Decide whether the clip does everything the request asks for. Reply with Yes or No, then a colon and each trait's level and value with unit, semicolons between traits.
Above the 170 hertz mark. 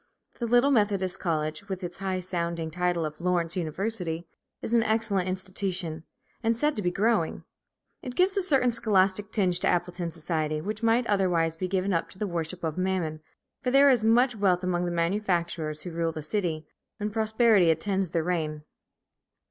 Yes: medium, 185 Hz